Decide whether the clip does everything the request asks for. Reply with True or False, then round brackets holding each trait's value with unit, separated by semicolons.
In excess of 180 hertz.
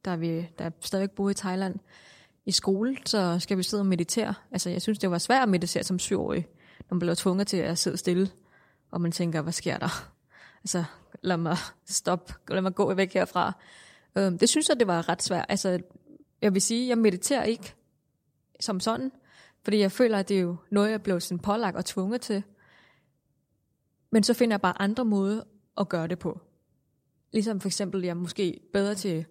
True (190 Hz)